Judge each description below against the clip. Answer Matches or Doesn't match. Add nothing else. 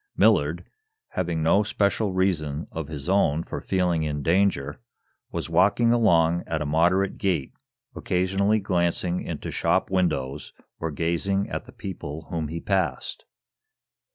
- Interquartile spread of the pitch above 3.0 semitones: Matches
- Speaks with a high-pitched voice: Doesn't match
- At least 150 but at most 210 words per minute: Doesn't match